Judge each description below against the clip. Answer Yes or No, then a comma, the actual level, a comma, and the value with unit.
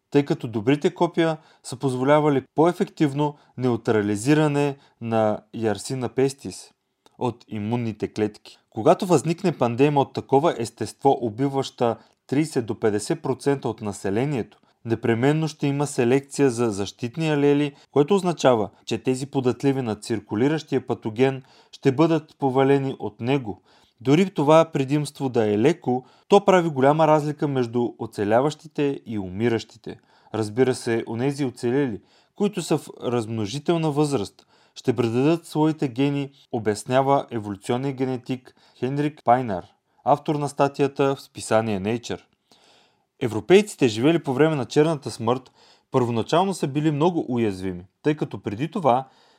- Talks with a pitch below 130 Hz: No, low, 135 Hz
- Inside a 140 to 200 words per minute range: No, average, 120 wpm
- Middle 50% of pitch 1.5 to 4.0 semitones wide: No, average, 4.4 semitones